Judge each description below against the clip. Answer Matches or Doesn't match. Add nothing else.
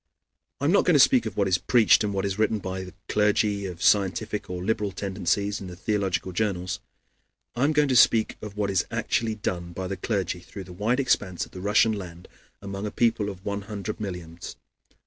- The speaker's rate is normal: Doesn't match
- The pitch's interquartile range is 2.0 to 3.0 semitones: Matches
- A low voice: Matches